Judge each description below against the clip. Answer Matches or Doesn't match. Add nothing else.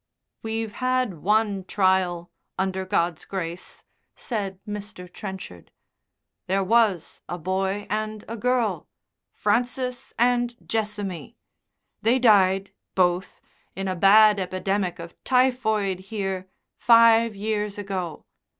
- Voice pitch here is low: Doesn't match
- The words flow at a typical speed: Doesn't match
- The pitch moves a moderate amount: Matches